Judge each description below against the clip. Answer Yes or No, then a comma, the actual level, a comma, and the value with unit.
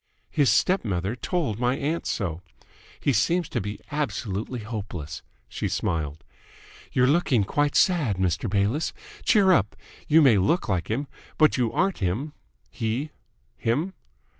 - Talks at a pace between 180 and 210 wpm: No, average, 140 wpm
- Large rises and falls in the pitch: Yes, wide, 7.2 semitones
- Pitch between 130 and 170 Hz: No, low, 120 Hz